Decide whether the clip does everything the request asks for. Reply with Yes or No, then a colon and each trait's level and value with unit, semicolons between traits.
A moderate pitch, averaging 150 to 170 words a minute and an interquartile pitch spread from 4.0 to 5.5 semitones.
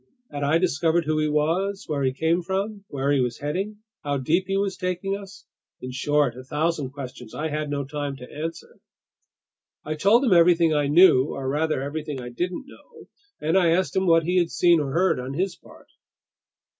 No: medium, 160 Hz; average, 195 wpm; average, 4.3 semitones